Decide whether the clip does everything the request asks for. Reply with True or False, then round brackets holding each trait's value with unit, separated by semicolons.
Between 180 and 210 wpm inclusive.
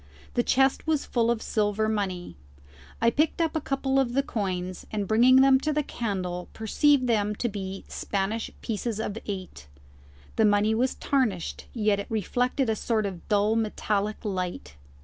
False (170 wpm)